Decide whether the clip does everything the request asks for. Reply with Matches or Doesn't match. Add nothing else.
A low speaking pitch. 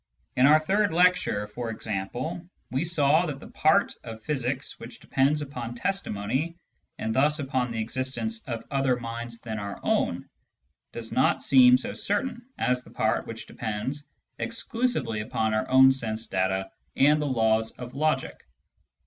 Matches